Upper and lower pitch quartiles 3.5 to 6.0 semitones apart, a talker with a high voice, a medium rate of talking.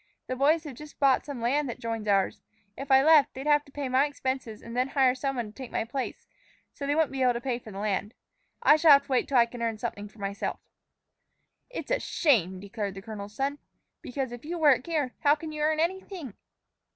No: average, 4.2 semitones; very high, 265 Hz; fast, 235 wpm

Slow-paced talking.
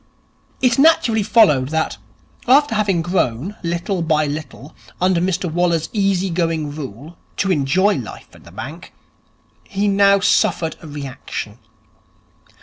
Yes: slow, 130 wpm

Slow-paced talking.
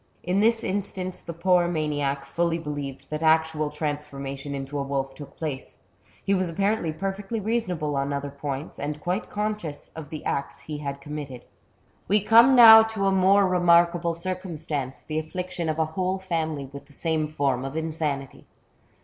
No: average, 165 wpm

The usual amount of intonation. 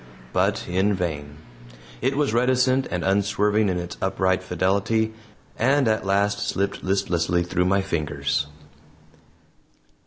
Yes: average, 3.4 semitones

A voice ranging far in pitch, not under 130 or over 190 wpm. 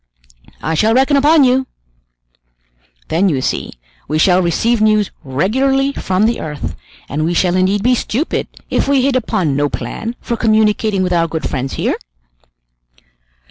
Yes: wide, 7.0 semitones; average, 155 wpm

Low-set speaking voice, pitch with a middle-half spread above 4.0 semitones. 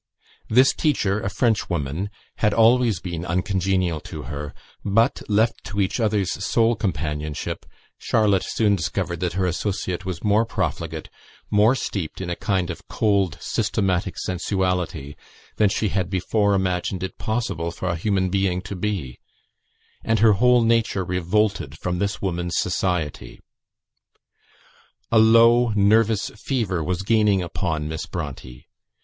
No: very low, 95 Hz; average, 3.6 semitones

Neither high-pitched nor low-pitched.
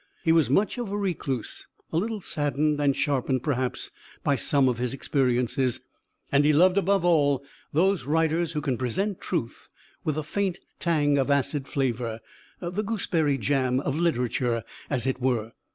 Yes: medium, 145 Hz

